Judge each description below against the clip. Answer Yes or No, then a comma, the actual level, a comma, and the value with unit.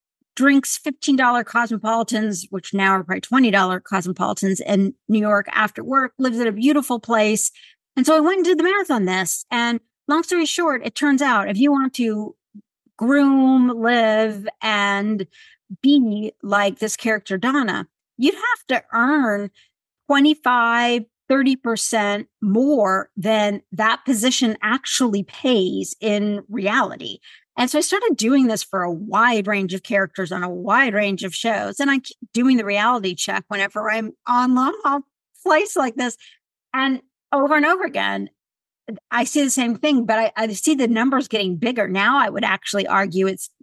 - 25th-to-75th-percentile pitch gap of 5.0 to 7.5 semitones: No, average, 4.6 semitones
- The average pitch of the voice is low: No, high, 230 Hz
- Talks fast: No, average, 160 wpm